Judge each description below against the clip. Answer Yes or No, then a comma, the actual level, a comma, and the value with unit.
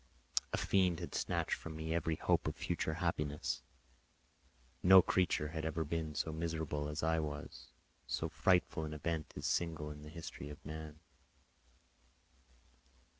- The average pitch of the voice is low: Yes, very low, 80 Hz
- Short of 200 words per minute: Yes, average, 145 wpm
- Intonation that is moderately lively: No, narrow, 1.6 semitones